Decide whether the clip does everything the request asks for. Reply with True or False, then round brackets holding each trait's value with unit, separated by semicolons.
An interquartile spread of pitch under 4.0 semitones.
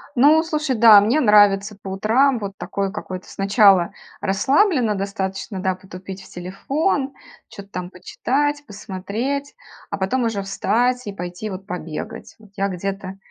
False (4.4 semitones)